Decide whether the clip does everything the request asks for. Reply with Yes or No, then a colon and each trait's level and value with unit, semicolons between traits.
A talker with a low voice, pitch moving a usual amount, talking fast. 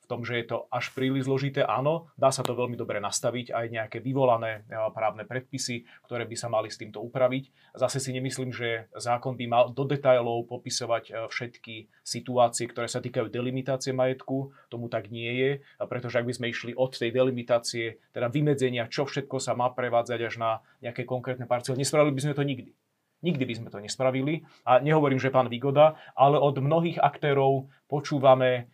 No: low, 125 Hz; narrow, 2.1 semitones; fast, 185 wpm